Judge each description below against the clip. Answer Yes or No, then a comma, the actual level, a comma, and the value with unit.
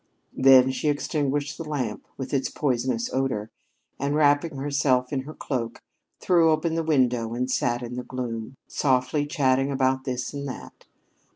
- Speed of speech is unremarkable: Yes, average, 160 wpm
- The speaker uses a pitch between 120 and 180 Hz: Yes, low, 135 Hz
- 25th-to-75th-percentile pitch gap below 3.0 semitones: Yes, narrow, 2.4 semitones